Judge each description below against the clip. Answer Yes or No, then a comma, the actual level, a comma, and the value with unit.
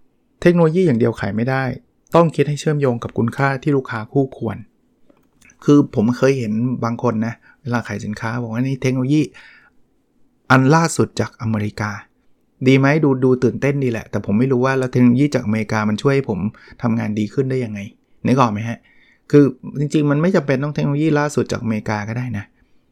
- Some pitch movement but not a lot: Yes, average, 3.7 semitones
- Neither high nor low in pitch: No, low, 125 Hz